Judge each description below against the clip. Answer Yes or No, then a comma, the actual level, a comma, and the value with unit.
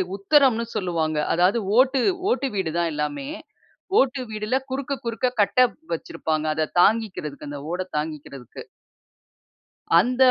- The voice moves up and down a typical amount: No, wide, 8.2 semitones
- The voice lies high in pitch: Yes, high, 200 Hz